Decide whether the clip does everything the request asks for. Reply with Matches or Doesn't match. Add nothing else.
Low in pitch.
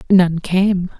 Doesn't match